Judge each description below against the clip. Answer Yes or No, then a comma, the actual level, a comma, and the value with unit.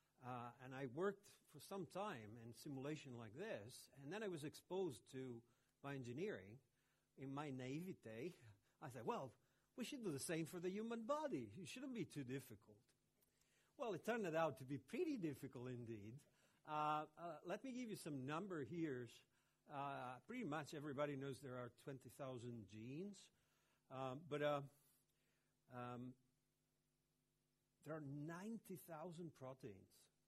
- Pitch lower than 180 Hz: Yes, medium, 140 Hz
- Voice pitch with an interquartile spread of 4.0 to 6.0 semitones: Yes, average, 5.3 semitones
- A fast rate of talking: No, average, 145 wpm